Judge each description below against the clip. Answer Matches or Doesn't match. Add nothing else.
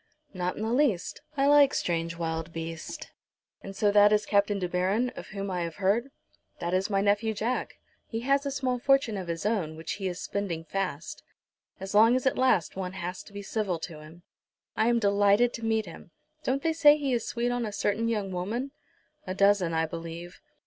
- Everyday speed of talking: Doesn't match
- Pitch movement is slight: Doesn't match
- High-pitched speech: Matches